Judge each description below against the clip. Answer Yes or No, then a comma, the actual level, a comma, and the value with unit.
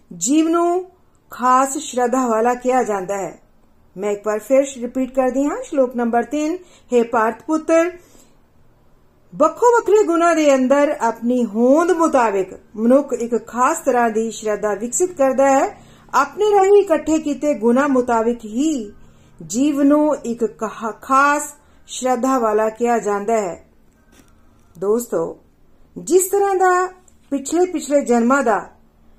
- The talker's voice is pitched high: Yes, very high, 260 Hz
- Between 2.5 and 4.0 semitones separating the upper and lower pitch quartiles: No, average, 5.2 semitones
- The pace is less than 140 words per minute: Yes, average, 125 wpm